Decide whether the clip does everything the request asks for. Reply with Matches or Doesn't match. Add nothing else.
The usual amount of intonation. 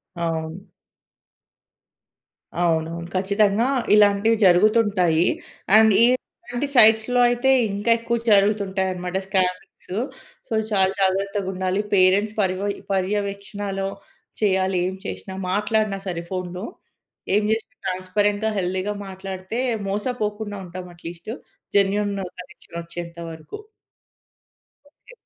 Doesn't match